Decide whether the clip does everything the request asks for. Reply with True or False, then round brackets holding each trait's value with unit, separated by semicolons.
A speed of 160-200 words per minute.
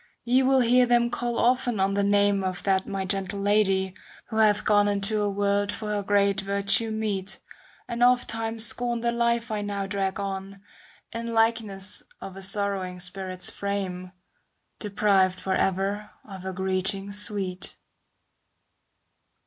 False (150 wpm)